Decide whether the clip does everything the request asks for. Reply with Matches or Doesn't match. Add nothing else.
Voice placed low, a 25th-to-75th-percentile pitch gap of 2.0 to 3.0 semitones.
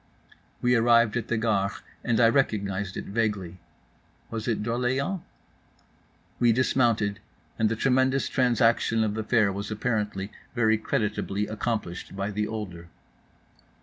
Matches